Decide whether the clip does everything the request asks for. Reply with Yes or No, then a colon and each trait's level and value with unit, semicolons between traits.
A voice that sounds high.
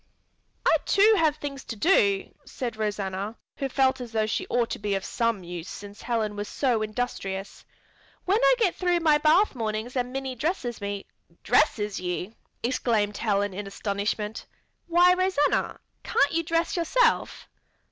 Yes: high, 235 Hz